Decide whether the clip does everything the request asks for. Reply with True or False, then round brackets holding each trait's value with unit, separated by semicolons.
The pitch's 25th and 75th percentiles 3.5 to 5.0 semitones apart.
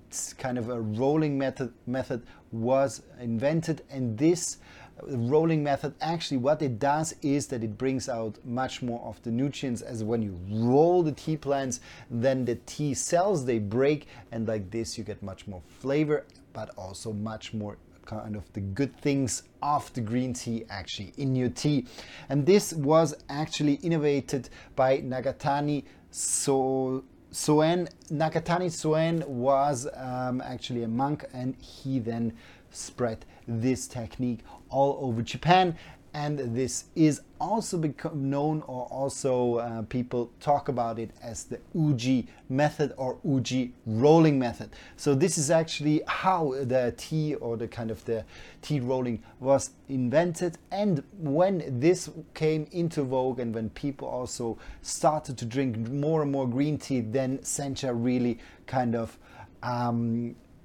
True (4.0 semitones)